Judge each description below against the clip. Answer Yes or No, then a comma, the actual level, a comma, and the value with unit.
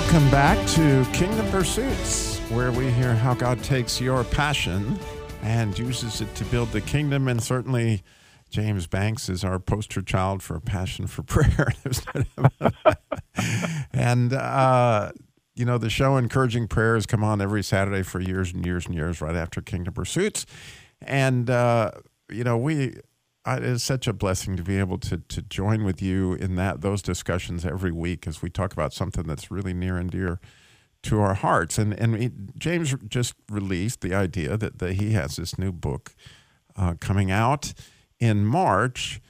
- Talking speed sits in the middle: Yes, average, 170 wpm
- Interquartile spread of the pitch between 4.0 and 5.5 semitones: Yes, average, 4.8 semitones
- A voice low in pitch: Yes, low, 105 Hz